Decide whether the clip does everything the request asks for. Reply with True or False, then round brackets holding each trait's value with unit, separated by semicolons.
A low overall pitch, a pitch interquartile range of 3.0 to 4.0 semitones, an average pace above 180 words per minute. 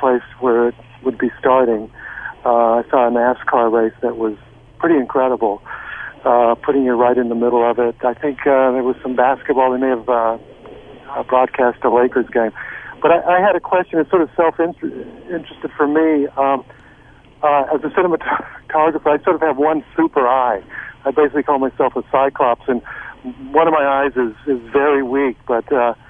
True (130 Hz; 3.7 semitones; 190 wpm)